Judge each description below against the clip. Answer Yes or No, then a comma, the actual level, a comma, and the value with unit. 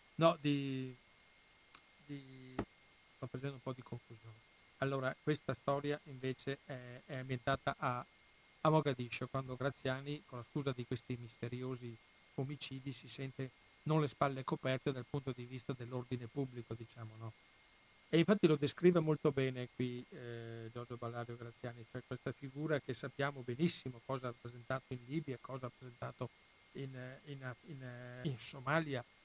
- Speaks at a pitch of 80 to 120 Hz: No, low, 130 Hz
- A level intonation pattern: Yes, narrow, 2.3 semitones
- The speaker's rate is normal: Yes, average, 150 wpm